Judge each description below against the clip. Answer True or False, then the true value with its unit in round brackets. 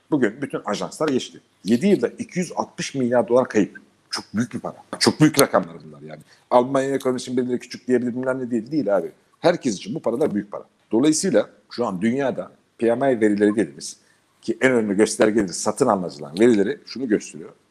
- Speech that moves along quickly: True (175 wpm)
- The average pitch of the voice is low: True (125 Hz)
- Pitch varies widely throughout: False (3.7 semitones)